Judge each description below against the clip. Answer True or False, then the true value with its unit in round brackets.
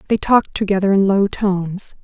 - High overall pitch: True (195 Hz)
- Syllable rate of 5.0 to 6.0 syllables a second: True (5.6 syllables/s)